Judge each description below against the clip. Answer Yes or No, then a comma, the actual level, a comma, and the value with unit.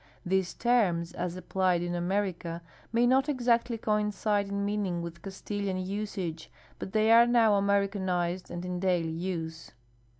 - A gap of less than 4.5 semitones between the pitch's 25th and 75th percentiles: Yes, average, 3.3 semitones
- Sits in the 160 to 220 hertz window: Yes, high, 190 Hz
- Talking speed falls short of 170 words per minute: Yes, average, 140 wpm